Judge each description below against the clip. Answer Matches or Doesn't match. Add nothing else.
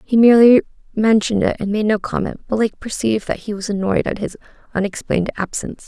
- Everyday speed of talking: Matches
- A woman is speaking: Matches